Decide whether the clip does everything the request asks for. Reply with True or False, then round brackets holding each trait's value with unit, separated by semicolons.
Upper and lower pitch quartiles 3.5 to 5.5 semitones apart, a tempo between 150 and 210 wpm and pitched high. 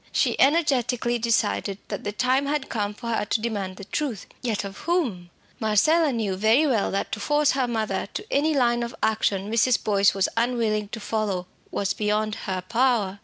True (3.8 semitones; 185 wpm; 225 Hz)